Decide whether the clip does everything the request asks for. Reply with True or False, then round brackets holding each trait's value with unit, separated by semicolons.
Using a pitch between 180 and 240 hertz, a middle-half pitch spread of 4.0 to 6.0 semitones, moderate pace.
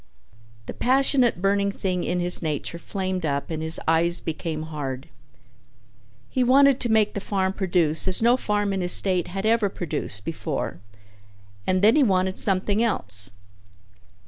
True (185 Hz; 4.3 semitones; 155 wpm)